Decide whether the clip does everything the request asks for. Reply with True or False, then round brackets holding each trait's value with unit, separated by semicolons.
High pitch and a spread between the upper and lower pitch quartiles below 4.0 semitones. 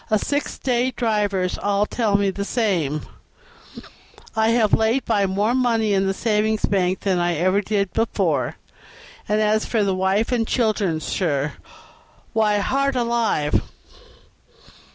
True (210 Hz; 2.9 semitones)